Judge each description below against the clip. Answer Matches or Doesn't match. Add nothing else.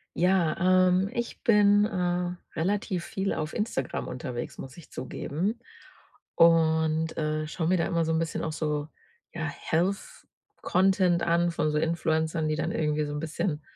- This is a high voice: Doesn't match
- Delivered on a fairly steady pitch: Doesn't match